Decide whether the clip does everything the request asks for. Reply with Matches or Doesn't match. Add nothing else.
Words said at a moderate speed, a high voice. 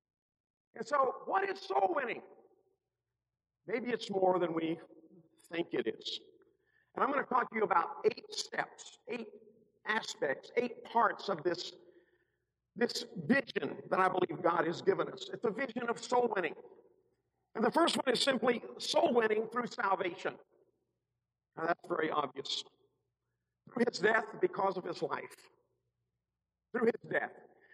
Matches